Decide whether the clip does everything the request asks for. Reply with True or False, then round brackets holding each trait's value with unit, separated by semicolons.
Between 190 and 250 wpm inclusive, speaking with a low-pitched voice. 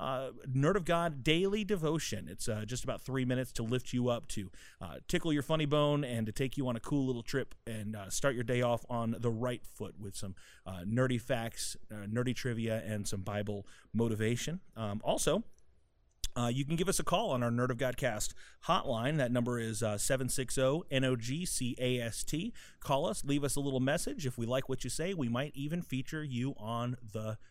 True (205 wpm; 125 Hz)